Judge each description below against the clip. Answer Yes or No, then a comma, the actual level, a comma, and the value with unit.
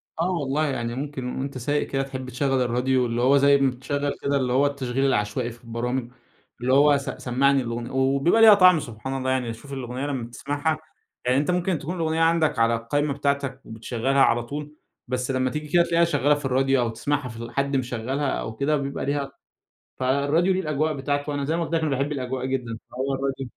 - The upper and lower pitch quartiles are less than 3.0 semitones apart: Yes, narrow, 2.4 semitones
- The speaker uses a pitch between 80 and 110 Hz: No, low, 135 Hz